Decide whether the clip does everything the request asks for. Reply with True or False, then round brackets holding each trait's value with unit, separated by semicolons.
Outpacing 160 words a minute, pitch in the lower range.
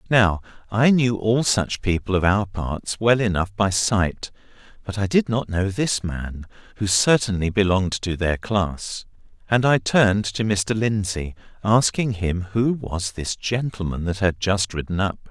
True (170 wpm; 100 Hz)